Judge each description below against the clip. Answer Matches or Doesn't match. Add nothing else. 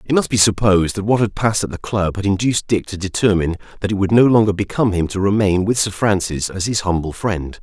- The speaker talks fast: Matches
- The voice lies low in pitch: Matches